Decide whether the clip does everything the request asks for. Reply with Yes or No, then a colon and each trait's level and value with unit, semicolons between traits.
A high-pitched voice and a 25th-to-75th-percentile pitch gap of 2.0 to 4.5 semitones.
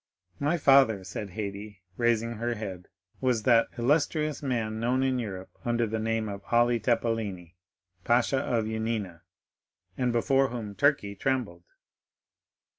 No: low, 115 Hz; average, 3.2 semitones